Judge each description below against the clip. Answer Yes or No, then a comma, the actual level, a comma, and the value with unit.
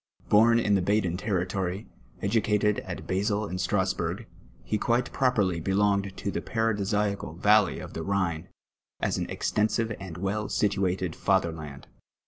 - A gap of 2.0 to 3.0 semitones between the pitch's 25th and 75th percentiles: Yes, narrow, 2.4 semitones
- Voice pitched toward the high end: No, low, 100 Hz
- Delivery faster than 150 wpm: No, average, 140 wpm